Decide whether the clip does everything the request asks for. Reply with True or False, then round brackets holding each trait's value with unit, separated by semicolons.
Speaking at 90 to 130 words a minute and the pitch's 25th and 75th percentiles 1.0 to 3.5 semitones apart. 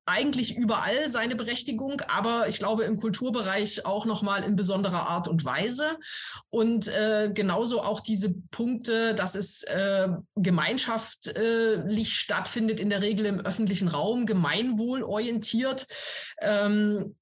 True (125 wpm; 2.5 semitones)